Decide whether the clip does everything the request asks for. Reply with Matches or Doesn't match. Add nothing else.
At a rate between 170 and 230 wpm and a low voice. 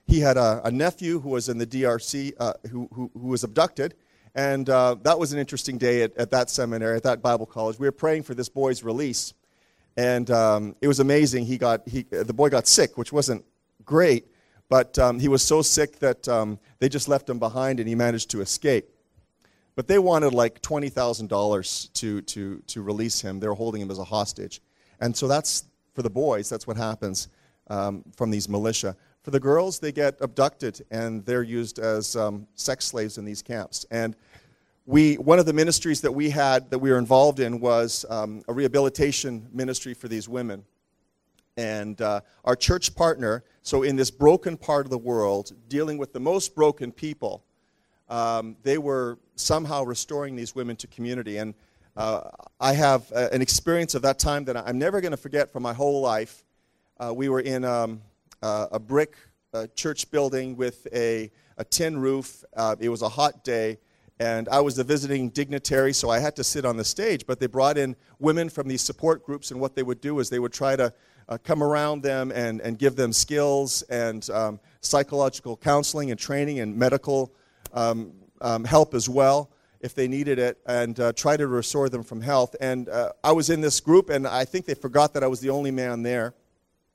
Matches